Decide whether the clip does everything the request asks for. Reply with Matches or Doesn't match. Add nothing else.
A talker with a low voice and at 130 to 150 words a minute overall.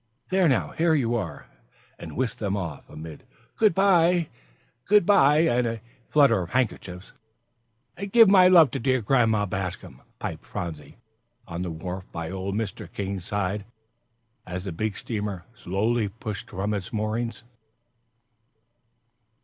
Matches